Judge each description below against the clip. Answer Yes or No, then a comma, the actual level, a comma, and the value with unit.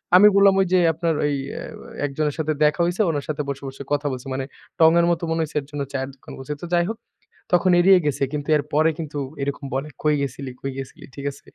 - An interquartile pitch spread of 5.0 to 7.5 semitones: No, average, 3.2 semitones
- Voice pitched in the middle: Yes, medium, 150 Hz